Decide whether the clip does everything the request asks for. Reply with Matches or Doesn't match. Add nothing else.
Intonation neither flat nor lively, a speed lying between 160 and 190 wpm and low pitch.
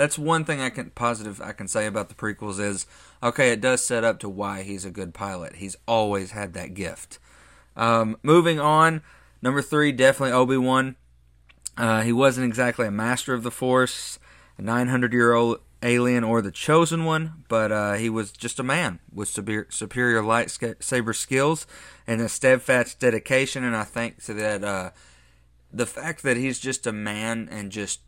Matches